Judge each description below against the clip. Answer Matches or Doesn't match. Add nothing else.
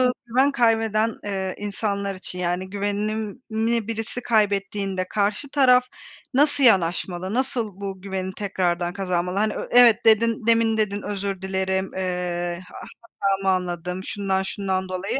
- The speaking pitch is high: Matches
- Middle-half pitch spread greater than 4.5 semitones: Doesn't match